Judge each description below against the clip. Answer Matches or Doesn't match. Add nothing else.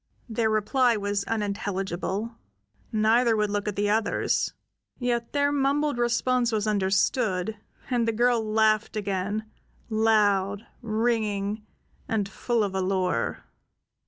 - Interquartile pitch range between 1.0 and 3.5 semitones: Matches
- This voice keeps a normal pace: Doesn't match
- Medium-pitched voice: Doesn't match